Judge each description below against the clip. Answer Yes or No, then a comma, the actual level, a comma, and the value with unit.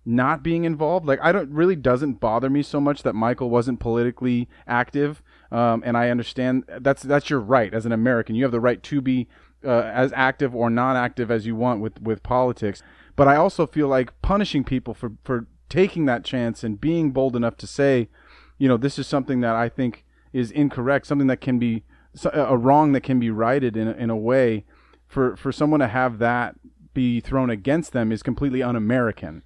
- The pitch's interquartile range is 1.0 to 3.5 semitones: Yes, average, 3.0 semitones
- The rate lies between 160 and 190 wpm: No, fast, 205 wpm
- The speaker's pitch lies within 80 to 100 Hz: No, low, 125 Hz